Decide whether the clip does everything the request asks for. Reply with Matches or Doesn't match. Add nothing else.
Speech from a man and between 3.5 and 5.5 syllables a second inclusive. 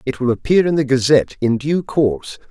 Doesn't match